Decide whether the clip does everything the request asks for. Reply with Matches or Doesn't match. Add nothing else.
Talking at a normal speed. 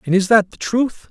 Doesn't match